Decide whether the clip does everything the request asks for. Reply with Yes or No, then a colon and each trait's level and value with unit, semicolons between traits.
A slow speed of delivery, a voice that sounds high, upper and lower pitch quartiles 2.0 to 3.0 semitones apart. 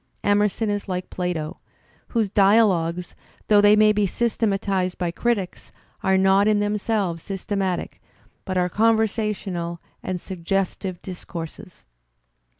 Yes: slow, 115 wpm; high, 195 Hz; narrow, 2.6 semitones